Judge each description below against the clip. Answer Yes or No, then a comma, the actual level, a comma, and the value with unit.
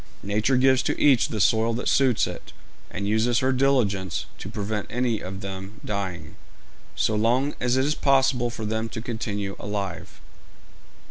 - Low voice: Yes, low, 110 Hz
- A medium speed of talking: Yes, average, 160 wpm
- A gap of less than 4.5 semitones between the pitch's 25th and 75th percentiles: Yes, average, 3.9 semitones